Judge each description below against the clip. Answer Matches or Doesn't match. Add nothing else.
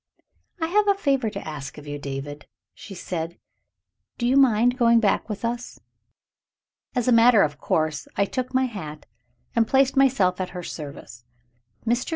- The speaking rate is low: Doesn't match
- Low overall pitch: Doesn't match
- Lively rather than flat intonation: Matches